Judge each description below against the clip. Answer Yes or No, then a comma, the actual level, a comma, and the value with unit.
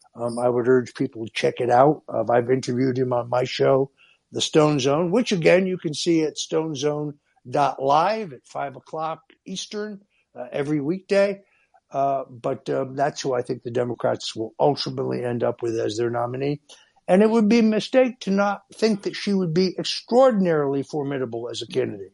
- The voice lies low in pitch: No, medium, 145 Hz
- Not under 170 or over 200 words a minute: Yes, average, 185 wpm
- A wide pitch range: Yes, wide, 6.9 semitones